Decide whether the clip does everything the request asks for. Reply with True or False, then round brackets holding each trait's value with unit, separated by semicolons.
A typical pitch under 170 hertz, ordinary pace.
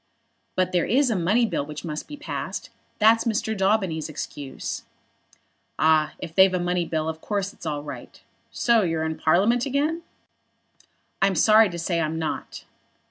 False (180 Hz; 165 wpm)